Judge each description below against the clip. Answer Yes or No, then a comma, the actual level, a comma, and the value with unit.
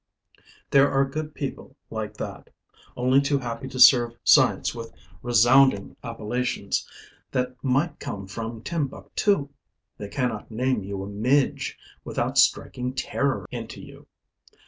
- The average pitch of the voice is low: Yes, low, 125 Hz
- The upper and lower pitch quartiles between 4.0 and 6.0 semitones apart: No, average, 3.1 semitones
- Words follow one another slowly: Yes, slow, 125 wpm